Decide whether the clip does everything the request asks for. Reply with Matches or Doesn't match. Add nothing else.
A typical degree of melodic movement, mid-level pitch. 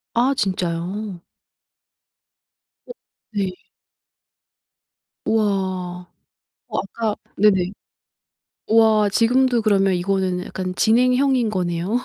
Doesn't match